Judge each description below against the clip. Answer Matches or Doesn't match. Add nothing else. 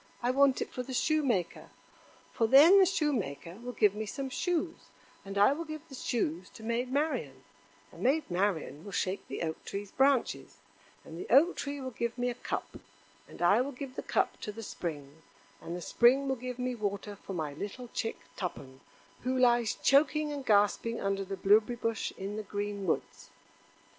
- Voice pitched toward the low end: Doesn't match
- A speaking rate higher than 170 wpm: Matches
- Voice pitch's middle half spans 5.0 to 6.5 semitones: Matches